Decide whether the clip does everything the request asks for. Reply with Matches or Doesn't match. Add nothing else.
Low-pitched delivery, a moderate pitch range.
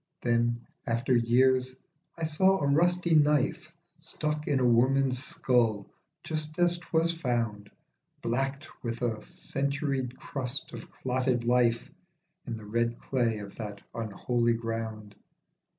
Matches